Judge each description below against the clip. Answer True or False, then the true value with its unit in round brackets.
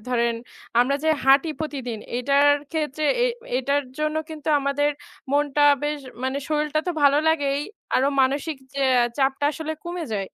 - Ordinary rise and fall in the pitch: False (2.2 semitones)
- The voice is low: False (285 Hz)